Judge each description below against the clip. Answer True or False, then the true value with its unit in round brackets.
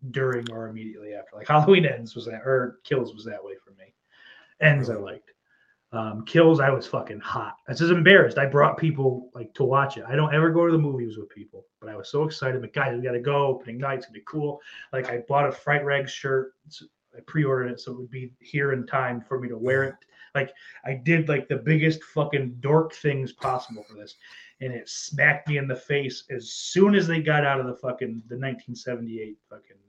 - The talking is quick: True (235 wpm)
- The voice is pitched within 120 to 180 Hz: True (135 Hz)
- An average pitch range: True (3.3 semitones)